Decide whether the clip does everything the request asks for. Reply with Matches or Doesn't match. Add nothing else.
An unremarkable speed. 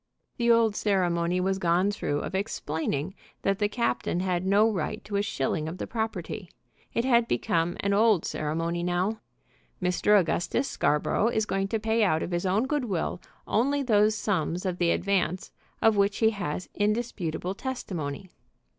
Matches